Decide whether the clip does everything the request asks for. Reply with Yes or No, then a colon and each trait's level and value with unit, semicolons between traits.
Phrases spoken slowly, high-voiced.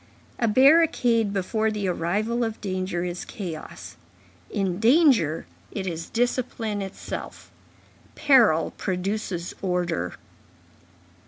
Yes: slow, 95 wpm; high, 205 Hz